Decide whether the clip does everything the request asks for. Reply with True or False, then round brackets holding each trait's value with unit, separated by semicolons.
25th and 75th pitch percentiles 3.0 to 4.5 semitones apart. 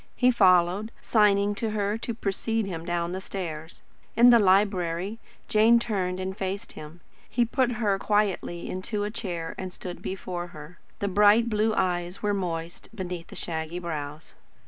True (3.5 semitones)